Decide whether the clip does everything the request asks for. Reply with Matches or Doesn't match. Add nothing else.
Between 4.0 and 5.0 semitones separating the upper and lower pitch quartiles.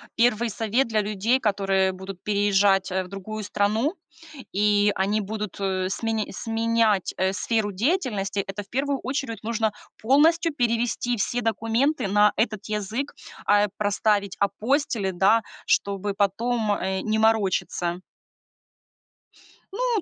Doesn't match